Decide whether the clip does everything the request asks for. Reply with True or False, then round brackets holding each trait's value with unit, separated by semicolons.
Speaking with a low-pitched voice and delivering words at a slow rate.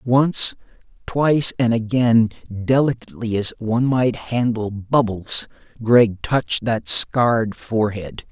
True (115 Hz; 110 wpm)